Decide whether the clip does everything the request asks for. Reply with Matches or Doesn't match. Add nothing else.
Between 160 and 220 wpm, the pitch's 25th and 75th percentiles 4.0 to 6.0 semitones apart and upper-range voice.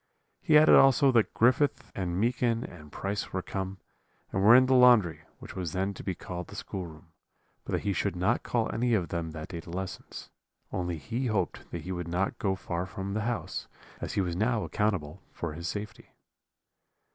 Doesn't match